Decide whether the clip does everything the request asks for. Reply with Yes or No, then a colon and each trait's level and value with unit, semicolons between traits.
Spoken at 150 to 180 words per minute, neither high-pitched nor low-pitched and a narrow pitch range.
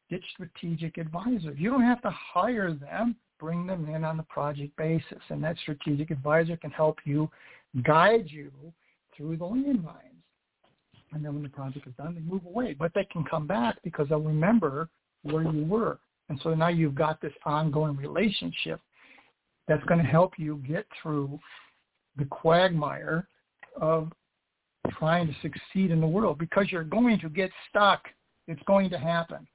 No: average, 170 wpm; medium, 165 Hz; average, 3.5 semitones